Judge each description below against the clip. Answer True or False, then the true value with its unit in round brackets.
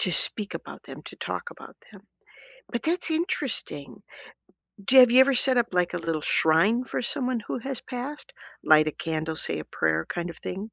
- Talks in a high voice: True (230 Hz)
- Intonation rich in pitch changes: True (8.1 semitones)